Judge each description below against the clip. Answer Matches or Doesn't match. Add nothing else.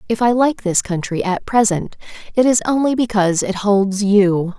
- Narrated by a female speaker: Matches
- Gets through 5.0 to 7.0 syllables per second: Doesn't match